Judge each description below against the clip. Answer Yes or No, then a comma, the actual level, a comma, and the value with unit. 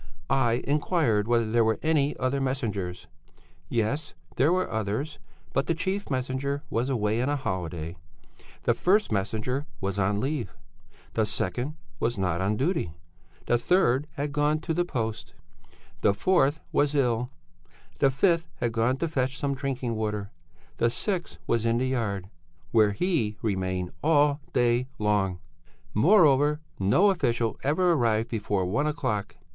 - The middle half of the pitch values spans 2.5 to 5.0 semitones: No, wide, 5.5 semitones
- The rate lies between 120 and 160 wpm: Yes, average, 150 wpm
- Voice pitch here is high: No, low, 125 Hz